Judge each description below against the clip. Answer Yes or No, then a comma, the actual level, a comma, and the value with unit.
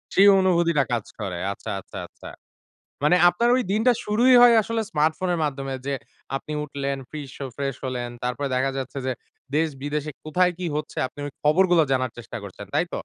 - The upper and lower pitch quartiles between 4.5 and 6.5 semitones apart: Yes, average, 4.8 semitones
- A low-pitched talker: No, medium, 150 Hz